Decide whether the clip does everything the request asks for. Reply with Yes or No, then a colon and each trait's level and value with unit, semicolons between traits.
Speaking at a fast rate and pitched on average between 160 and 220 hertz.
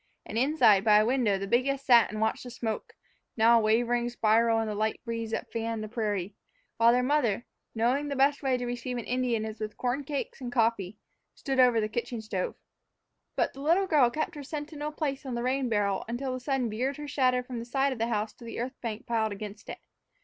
No: fast, 230 wpm; high, 240 Hz